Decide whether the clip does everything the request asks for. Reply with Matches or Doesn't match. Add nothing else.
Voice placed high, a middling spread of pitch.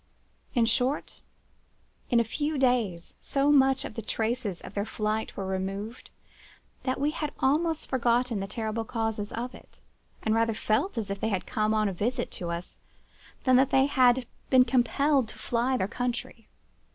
Matches